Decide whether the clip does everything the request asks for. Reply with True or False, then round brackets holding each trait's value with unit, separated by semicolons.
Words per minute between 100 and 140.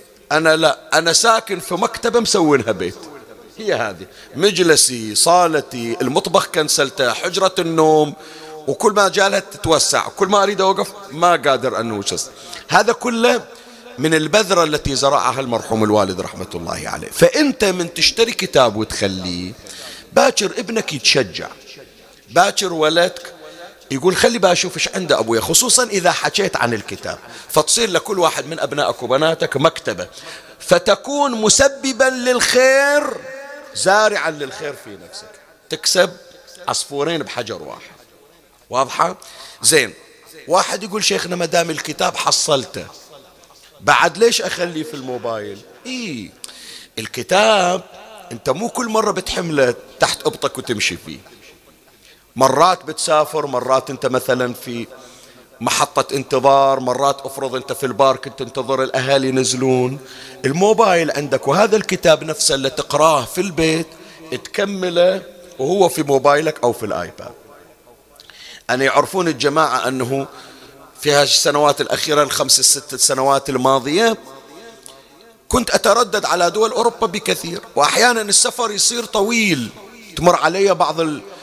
True (115 wpm)